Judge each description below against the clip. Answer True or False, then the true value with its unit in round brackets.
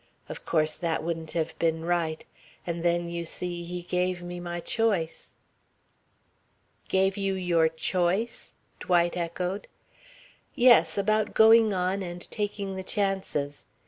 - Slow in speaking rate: True (130 wpm)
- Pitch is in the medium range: True (175 Hz)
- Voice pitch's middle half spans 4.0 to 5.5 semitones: False (2.4 semitones)